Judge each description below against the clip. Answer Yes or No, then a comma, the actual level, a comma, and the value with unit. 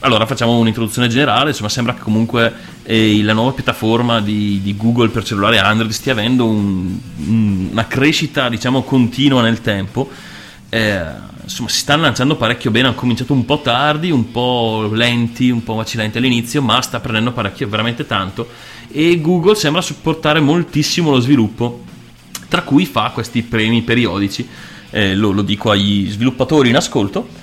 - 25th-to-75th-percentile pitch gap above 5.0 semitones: No, average, 3.3 semitones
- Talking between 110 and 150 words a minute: No, average, 160 wpm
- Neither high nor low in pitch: No, low, 120 Hz